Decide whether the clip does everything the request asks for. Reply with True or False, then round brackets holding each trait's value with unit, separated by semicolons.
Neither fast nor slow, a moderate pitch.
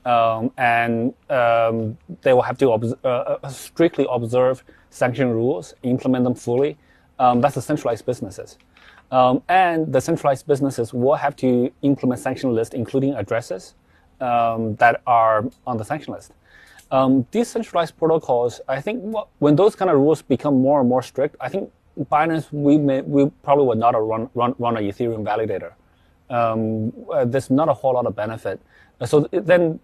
False (170 wpm; 130 Hz)